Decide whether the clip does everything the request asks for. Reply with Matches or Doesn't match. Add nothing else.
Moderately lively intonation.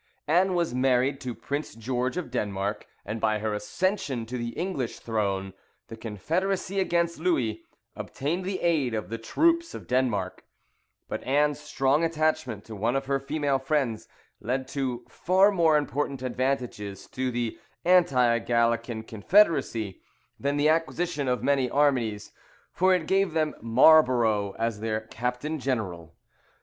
Doesn't match